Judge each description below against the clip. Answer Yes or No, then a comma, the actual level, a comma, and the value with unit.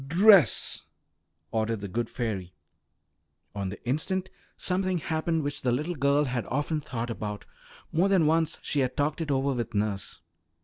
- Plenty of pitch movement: Yes, wide, 6.0 semitones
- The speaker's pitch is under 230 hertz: Yes, medium, 140 Hz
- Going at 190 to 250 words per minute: No, average, 160 wpm